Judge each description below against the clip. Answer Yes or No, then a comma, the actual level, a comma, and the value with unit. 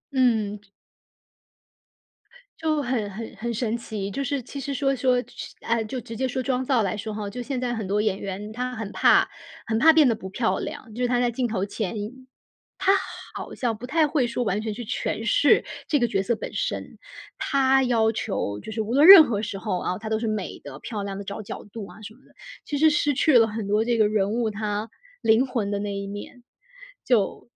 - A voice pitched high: Yes, high, 225 Hz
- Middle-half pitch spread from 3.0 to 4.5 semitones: Yes, average, 3.5 semitones